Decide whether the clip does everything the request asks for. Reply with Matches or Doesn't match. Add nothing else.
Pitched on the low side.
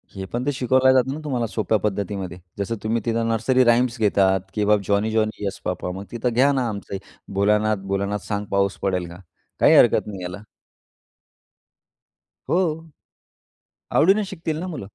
Matches